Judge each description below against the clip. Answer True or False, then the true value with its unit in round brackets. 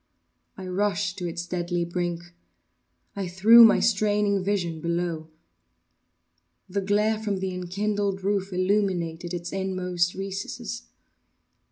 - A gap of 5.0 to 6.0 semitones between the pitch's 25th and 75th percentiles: False (2.6 semitones)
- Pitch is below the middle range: False (190 Hz)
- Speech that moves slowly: True (115 wpm)